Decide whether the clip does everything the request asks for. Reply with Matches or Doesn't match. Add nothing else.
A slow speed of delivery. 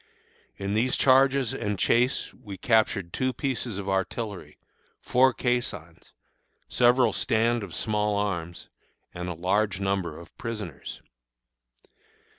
Matches